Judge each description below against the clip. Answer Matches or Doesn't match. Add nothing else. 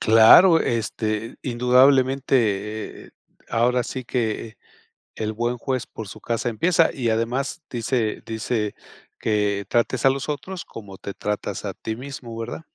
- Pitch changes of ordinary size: Matches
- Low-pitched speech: Matches